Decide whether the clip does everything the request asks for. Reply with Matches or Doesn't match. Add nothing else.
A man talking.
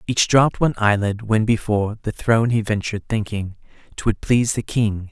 Matches